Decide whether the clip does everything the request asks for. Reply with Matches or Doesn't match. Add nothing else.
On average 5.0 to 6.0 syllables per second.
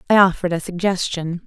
Doesn't match